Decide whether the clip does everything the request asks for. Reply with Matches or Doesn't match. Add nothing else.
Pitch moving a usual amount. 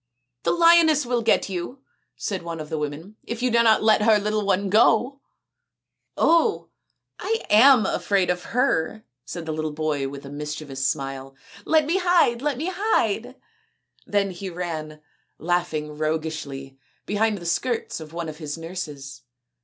Doesn't match